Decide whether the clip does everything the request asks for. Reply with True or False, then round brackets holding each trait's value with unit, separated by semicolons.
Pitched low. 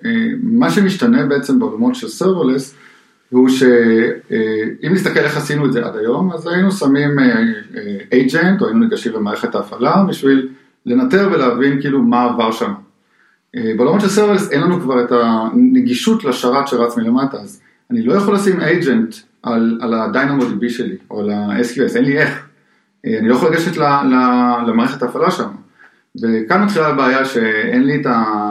False (145 Hz)